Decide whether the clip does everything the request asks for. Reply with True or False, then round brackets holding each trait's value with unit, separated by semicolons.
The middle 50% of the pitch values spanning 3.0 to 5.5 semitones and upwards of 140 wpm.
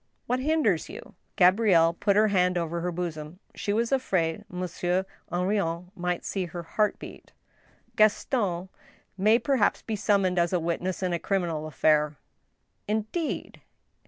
True (3.6 semitones; 160 wpm)